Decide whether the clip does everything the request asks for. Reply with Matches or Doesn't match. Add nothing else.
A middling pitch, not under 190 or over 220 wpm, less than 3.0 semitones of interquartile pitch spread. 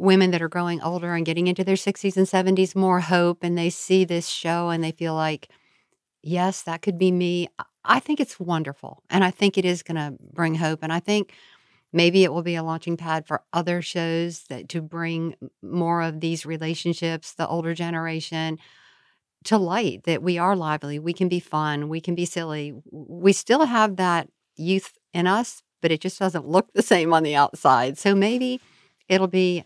Matches